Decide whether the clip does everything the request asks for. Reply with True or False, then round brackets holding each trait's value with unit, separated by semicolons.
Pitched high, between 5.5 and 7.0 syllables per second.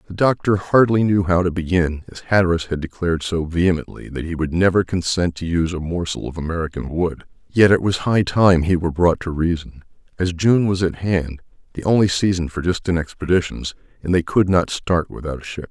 False (85 Hz; 5.6 syllables/s)